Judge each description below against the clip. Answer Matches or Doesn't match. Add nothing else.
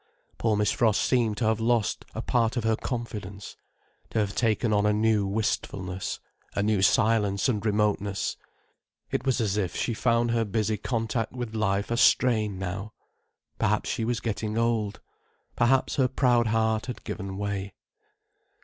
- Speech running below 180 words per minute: Matches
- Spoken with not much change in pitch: Matches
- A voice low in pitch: Matches